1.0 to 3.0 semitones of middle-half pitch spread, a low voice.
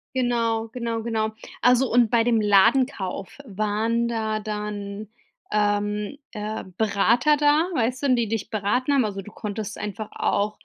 No: narrow, 2.5 semitones; high, 220 Hz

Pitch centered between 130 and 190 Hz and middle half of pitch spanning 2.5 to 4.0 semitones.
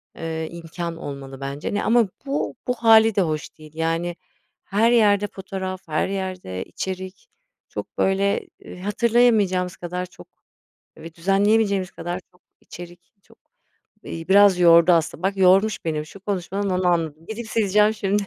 Yes: medium, 185 Hz; average, 3.4 semitones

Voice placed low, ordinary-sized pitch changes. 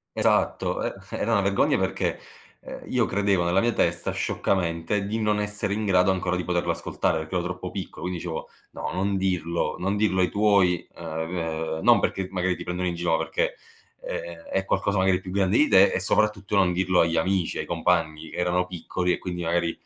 No: very low, 90 Hz; narrow, 2.3 semitones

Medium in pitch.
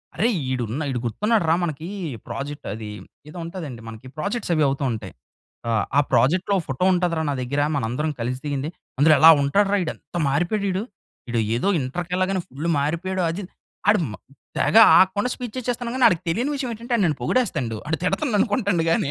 Yes: medium, 165 Hz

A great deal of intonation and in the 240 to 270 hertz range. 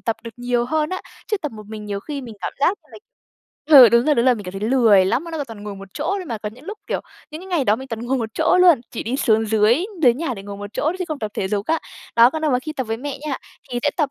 Yes: wide, 5.8 semitones; high, 245 Hz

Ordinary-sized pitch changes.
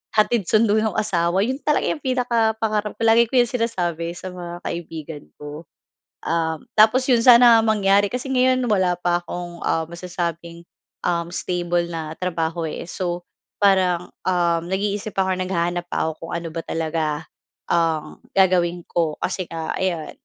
Yes: average, 4.2 semitones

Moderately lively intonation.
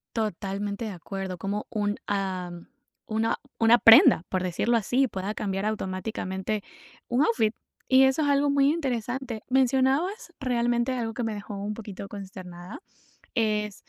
Yes: average, 4.1 semitones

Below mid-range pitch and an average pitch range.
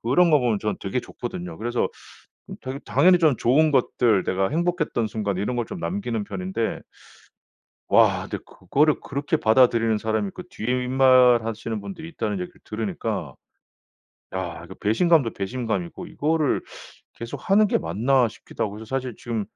Yes: low, 115 Hz; average, 4.7 semitones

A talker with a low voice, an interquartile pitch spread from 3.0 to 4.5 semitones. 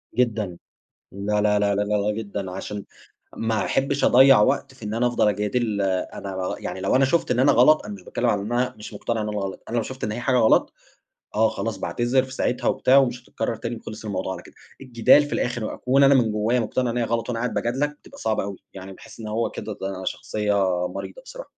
Yes: low, 110 Hz; average, 3.4 semitones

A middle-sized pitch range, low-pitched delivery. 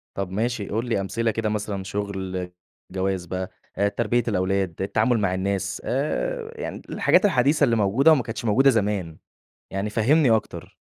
Yes: average, 4.0 semitones; low, 105 Hz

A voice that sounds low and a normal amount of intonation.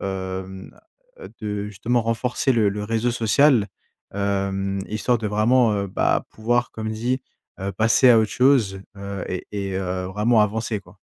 Yes: low, 105 Hz; average, 3.1 semitones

